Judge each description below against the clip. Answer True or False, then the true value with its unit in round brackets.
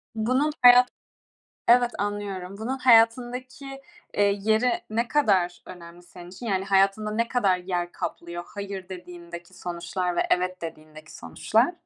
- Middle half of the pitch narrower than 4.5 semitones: False (4.9 semitones)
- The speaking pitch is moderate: False (195 Hz)